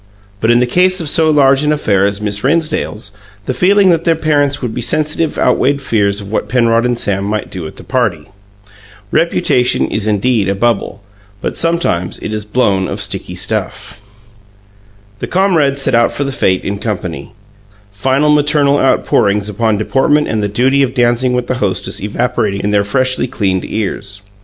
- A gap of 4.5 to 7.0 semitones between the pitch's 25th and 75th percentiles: Yes, wide, 5.6 semitones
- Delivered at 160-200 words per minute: Yes, average, 180 wpm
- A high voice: No, low, 120 Hz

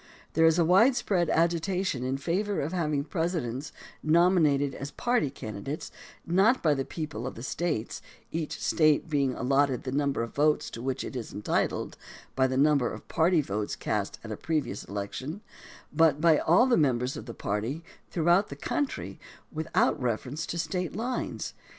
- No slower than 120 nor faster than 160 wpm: No, average, 170 wpm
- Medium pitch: Yes, medium, 150 Hz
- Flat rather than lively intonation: No, average, 4.6 semitones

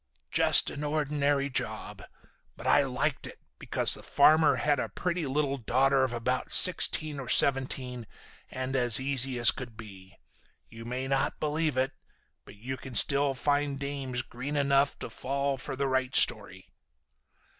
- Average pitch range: No, narrow, 2.2 semitones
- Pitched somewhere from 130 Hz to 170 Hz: Yes, low, 135 Hz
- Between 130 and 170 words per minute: Yes, average, 155 wpm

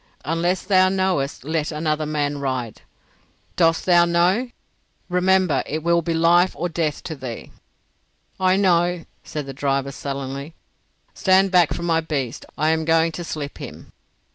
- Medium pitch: Yes, medium, 165 Hz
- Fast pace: No, average, 150 wpm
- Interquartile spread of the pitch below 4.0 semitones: Yes, average, 3.4 semitones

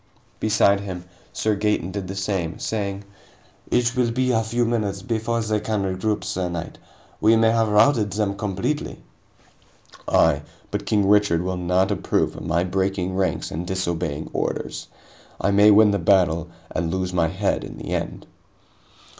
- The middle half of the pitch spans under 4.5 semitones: Yes, average, 2.9 semitones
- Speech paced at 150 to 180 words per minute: Yes, average, 165 wpm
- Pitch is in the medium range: No, low, 100 Hz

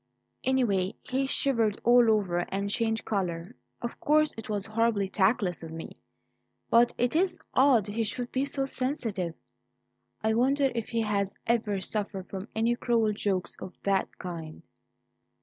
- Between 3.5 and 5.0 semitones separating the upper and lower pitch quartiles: Yes, average, 3.9 semitones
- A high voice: Yes, high, 220 Hz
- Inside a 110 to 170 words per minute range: Yes, average, 150 wpm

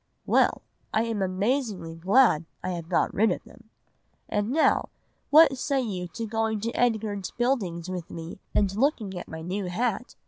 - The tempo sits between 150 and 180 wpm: Yes, average, 170 wpm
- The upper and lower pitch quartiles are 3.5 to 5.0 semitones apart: Yes, average, 4.5 semitones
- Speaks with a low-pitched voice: No, high, 210 Hz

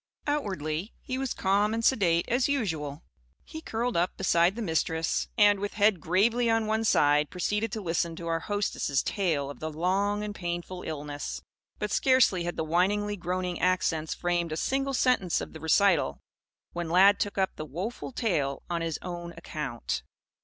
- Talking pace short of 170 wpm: No, average, 175 wpm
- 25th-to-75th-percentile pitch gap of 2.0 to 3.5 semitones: No, average, 4.4 semitones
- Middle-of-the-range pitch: Yes, medium, 180 Hz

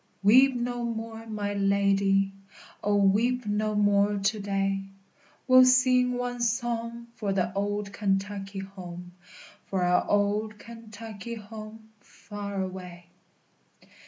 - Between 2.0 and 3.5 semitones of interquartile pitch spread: Yes, narrow, 2.6 semitones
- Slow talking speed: Yes, slow, 120 wpm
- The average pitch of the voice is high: Yes, high, 205 Hz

